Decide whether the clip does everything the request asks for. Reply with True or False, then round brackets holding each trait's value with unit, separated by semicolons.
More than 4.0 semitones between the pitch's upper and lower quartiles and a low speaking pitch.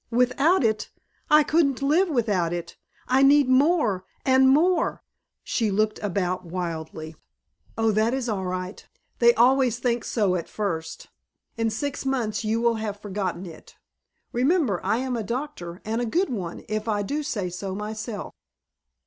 False (5.4 semitones; 225 Hz)